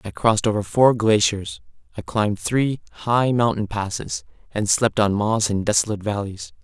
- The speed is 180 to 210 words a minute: No, average, 165 wpm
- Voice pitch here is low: Yes, low, 110 Hz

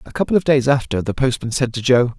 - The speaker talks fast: Yes, fast, 275 wpm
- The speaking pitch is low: Yes, low, 130 Hz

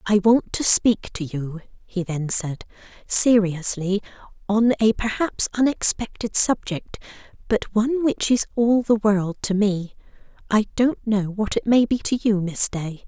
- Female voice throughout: Yes, female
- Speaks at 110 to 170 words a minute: Yes, average, 150 wpm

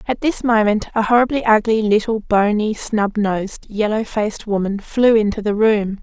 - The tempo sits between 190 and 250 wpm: No, average, 170 wpm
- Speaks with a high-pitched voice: Yes, high, 215 Hz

